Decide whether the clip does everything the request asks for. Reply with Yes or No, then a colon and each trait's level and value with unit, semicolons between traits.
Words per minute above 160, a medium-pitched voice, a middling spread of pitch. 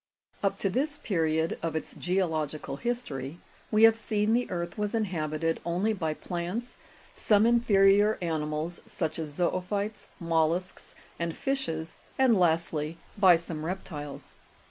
No: slow, 135 wpm; medium, 175 Hz; average, 4.6 semitones